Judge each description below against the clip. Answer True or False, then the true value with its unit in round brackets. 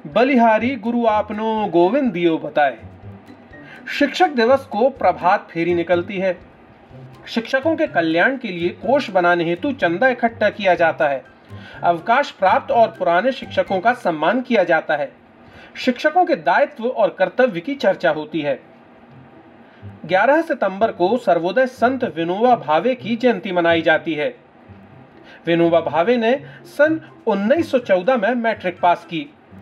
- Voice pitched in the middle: False (210 Hz)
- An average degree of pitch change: False (7.1 semitones)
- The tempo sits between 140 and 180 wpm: False (130 wpm)